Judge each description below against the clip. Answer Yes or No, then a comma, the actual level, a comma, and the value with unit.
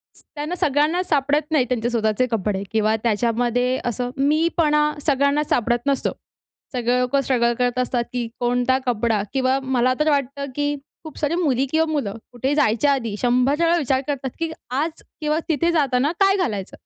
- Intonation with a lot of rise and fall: No, average, 3.6 semitones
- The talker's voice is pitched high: Yes, very high, 265 Hz